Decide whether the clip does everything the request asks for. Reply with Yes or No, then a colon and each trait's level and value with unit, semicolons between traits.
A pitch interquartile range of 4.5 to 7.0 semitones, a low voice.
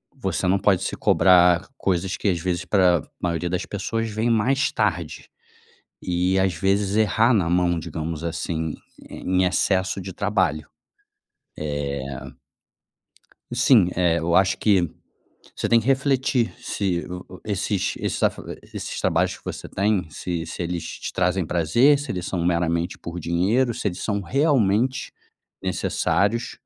No: average, 3.5 semitones; very low, 95 Hz